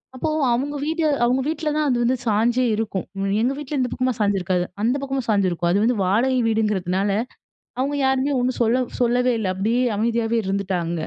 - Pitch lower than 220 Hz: No, high, 235 Hz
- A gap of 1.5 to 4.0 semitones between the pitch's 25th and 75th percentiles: No, average, 4.5 semitones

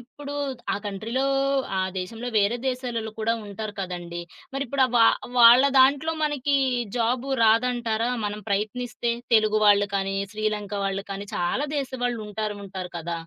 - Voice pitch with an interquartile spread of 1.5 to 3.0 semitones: No, average, 3.6 semitones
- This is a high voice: Yes, high, 220 Hz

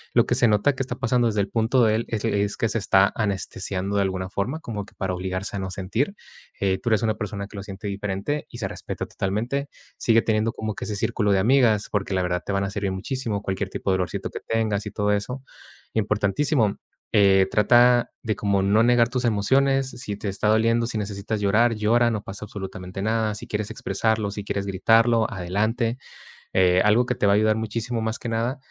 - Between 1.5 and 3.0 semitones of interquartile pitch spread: Yes, average, 2.7 semitones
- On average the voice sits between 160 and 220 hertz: No, low, 105 Hz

